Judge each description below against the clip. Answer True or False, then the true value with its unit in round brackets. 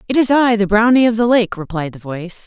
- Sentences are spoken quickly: True (270 wpm)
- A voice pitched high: True (210 Hz)